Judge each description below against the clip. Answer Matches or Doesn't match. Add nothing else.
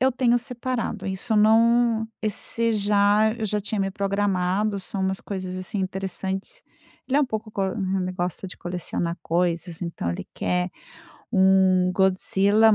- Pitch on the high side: Matches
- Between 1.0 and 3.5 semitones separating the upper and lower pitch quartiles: Matches